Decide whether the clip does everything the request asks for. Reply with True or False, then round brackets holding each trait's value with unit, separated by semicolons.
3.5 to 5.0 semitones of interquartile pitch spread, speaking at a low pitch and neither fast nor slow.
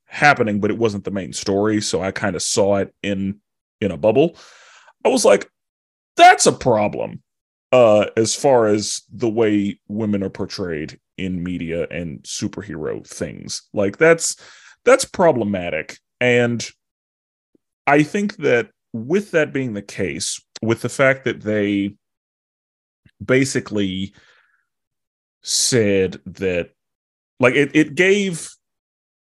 False (4.6 semitones; 105 Hz; 125 wpm)